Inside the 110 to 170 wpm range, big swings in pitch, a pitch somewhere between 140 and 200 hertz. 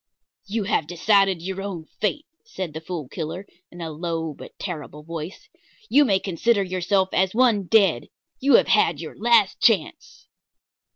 No: average, 160 wpm; average, 4.1 semitones; high, 190 Hz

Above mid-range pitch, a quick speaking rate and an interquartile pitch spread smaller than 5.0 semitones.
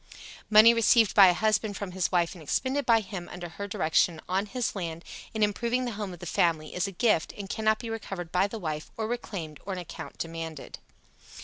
Yes: high, 195 Hz; fast, 215 wpm; average, 4.1 semitones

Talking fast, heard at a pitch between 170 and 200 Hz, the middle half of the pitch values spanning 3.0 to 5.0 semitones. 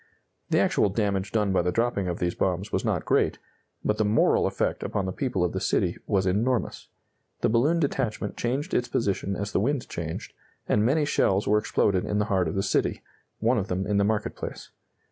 No: fast, 210 wpm; low, 105 Hz; average, 3.5 semitones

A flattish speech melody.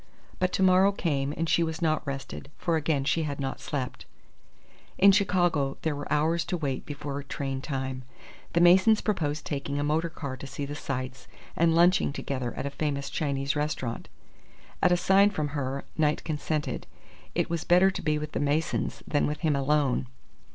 No: average, 3.2 semitones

